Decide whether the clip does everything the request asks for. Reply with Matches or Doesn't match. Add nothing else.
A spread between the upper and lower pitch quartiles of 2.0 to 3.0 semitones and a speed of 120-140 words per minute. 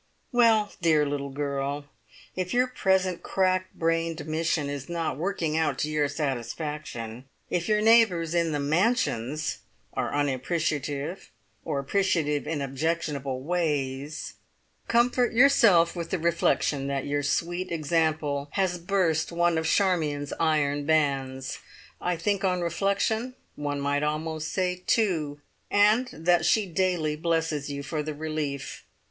Doesn't match